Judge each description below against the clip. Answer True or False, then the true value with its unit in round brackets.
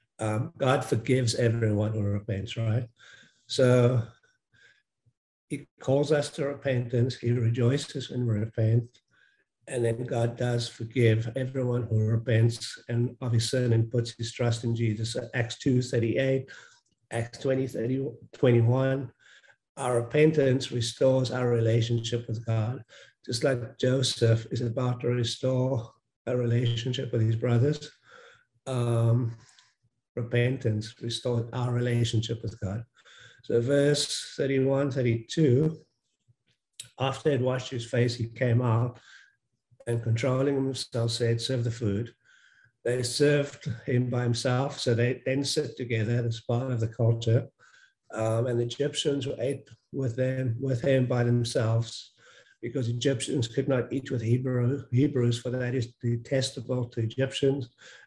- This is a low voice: True (120 Hz)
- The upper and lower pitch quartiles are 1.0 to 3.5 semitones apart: True (2.4 semitones)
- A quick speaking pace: False (135 wpm)